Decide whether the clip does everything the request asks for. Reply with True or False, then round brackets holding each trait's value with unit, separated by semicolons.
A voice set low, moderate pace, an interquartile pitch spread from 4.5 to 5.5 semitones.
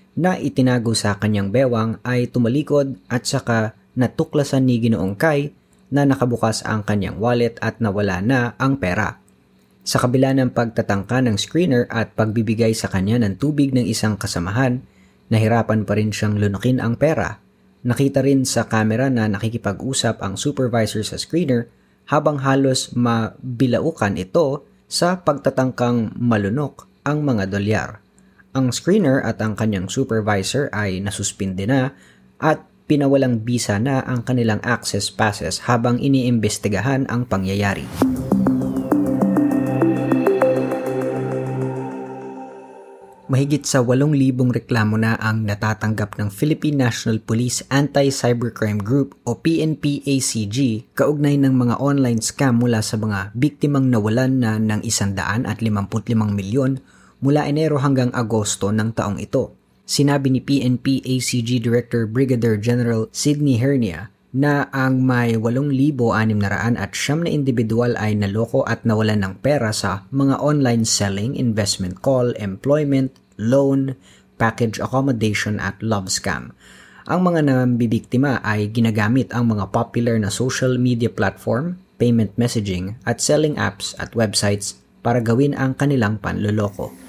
False (120 Hz; 125 wpm; 4.0 semitones)